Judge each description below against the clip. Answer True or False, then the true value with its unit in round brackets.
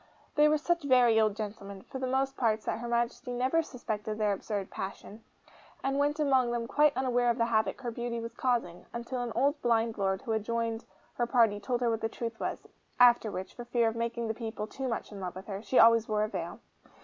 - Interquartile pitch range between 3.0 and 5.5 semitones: False (2.5 semitones)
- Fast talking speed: True (230 wpm)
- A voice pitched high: True (235 Hz)